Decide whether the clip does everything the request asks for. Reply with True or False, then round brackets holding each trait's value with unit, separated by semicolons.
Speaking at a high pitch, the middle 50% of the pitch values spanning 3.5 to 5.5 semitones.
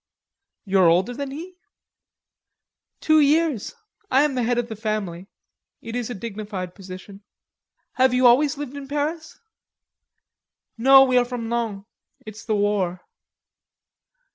True (235 Hz; 5.1 semitones)